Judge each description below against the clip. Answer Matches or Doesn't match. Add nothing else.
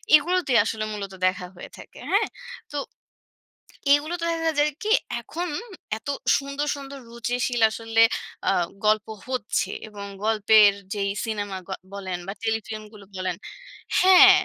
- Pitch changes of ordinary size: Doesn't match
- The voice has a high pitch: Matches